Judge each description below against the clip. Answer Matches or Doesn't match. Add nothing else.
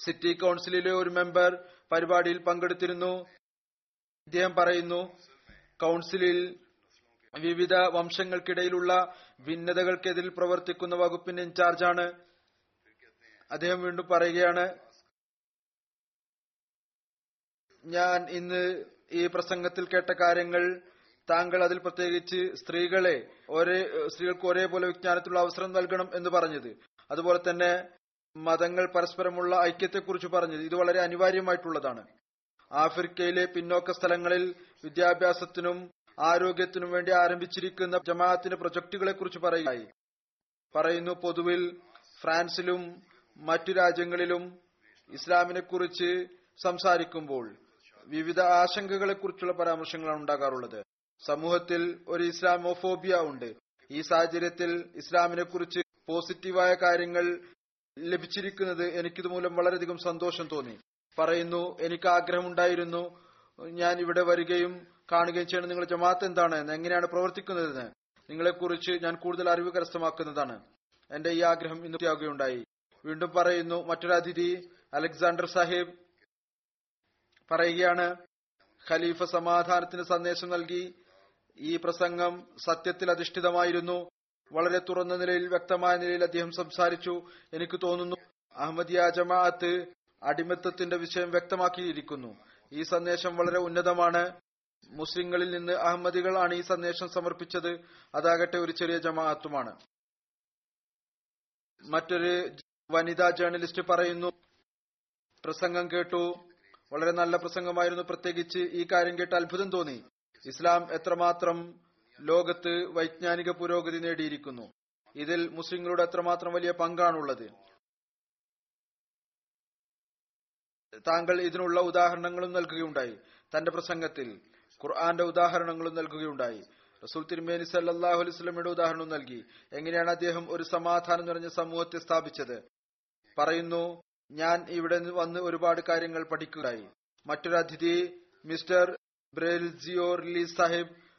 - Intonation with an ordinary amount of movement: Doesn't match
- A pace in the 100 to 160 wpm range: Doesn't match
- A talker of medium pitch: Matches